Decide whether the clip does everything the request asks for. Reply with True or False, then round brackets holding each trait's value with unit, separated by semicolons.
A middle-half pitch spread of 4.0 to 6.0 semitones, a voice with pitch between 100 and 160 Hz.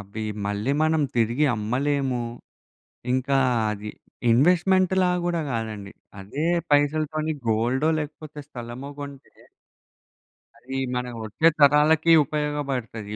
True (4.7 semitones; 140 Hz)